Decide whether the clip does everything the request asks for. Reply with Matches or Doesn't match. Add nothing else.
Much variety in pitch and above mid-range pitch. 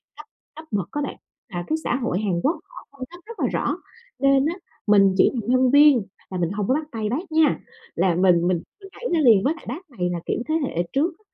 Matches